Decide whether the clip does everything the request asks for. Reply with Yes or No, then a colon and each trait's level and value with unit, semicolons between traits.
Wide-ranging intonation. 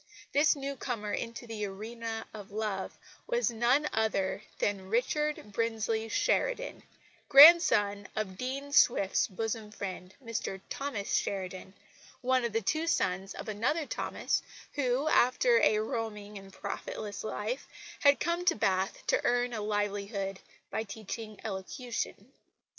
No: average, 4.1 semitones